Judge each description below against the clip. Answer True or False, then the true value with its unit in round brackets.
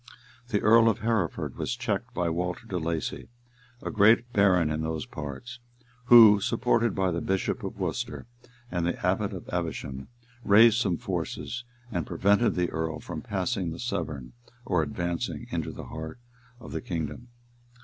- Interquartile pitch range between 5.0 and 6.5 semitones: True (5.4 semitones)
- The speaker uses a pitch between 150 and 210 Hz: False (95 Hz)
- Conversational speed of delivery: True (160 wpm)